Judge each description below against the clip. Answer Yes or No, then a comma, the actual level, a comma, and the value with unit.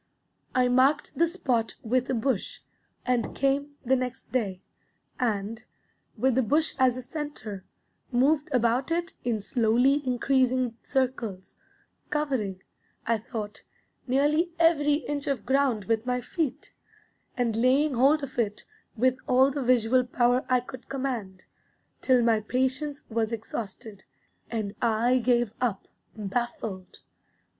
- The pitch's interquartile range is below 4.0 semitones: Yes, average, 3.1 semitones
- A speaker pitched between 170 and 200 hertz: No, very high, 250 Hz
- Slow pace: Yes, slow, 130 wpm